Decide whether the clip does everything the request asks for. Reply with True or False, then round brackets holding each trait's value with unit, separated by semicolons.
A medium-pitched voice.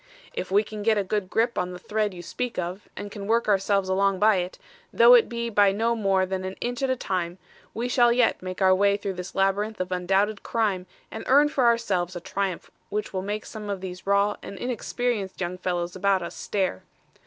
False (200 Hz)